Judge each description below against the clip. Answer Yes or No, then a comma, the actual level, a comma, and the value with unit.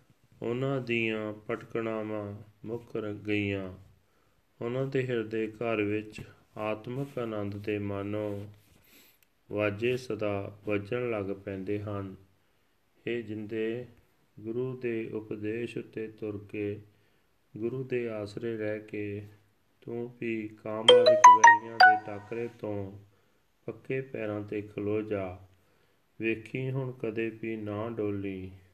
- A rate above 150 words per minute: No, average, 110 wpm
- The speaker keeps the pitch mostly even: Yes, narrow, 2.2 semitones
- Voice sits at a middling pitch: No, low, 110 Hz